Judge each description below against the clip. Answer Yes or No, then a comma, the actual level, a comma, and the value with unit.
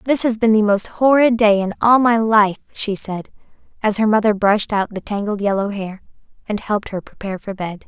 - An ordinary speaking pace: No, fast, 215 wpm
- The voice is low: No, high, 210 Hz